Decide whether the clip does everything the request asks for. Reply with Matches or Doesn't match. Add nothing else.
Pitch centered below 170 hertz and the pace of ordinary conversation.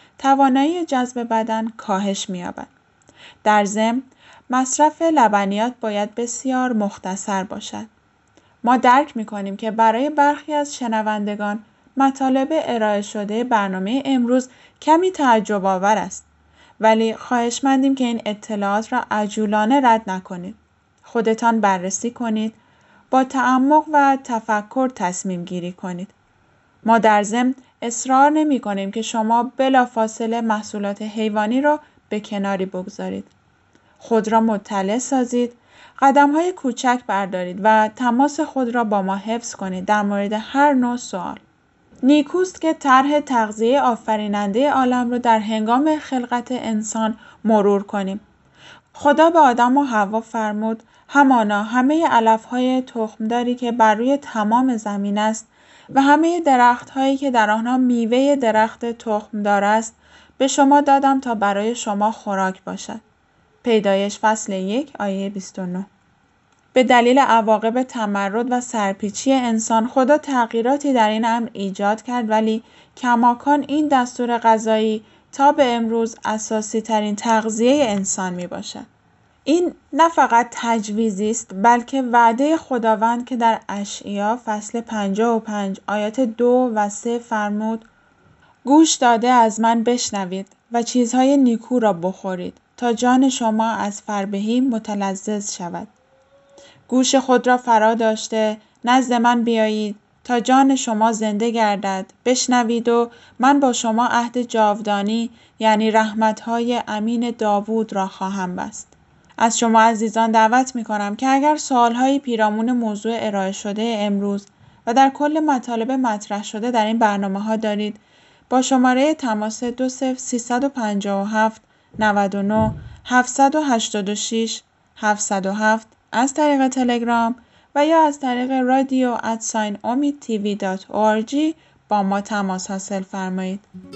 Doesn't match